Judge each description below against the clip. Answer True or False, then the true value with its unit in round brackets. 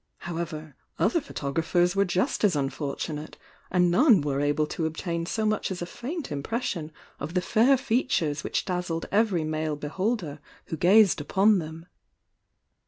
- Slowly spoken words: False (150 wpm)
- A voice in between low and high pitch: True (175 Hz)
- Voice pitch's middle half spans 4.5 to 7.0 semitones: True (5.2 semitones)